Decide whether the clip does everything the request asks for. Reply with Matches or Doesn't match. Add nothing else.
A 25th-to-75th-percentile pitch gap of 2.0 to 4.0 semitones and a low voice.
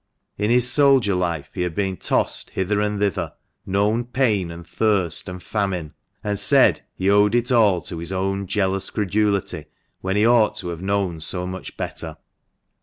Matches